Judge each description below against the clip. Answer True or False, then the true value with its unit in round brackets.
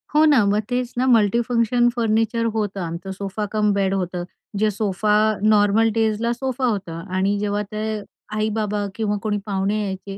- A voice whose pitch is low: False (210 Hz)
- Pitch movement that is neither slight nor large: False (2.3 semitones)